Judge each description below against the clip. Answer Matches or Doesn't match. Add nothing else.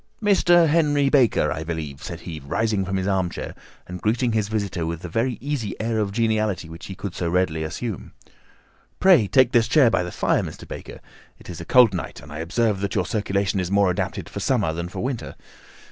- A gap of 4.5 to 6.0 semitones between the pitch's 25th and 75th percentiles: Matches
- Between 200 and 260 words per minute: Matches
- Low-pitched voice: Matches